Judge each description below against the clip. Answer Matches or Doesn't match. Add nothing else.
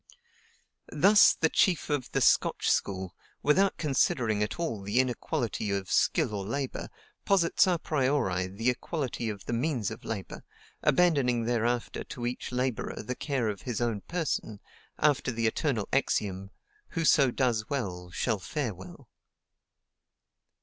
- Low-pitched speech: Matches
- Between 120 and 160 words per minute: Matches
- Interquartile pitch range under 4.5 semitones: Doesn't match